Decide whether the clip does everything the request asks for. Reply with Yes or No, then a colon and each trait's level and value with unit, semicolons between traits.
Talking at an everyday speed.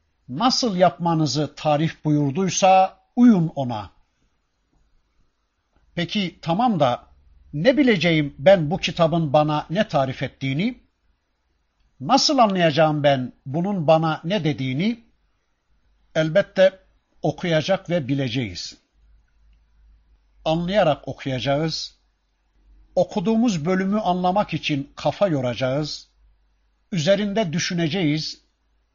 No: slow, 80 wpm